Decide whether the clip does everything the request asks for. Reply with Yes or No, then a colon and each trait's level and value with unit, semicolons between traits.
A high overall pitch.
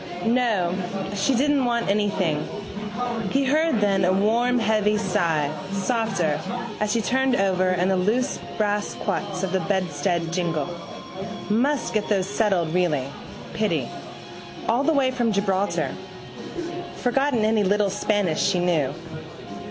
Yes: high, 205 Hz